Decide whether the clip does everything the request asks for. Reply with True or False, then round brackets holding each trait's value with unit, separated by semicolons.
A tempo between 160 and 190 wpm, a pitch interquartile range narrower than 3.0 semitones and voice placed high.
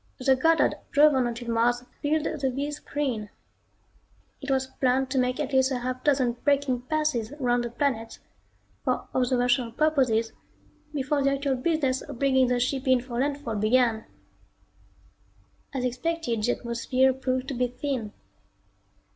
False (150 wpm; 2.5 semitones; 260 Hz)